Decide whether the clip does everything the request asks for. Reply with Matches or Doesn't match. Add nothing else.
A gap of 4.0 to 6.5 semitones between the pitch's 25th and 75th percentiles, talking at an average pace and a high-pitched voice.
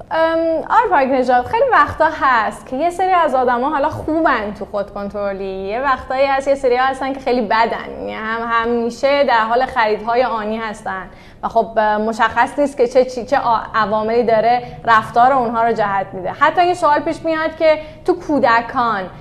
Doesn't match